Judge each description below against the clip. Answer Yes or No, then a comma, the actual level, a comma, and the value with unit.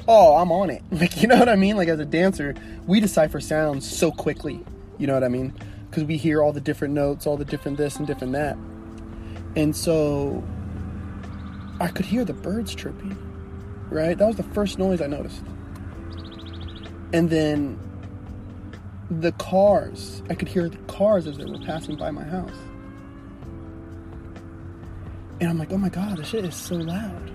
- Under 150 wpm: No, average, 180 wpm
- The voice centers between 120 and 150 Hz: Yes, medium, 140 Hz